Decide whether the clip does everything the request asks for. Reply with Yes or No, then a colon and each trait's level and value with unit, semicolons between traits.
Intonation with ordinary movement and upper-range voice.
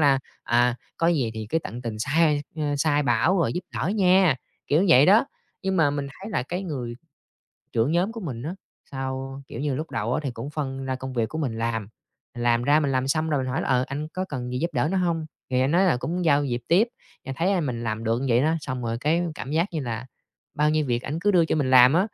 No: average, 4.7 semitones; medium, 140 Hz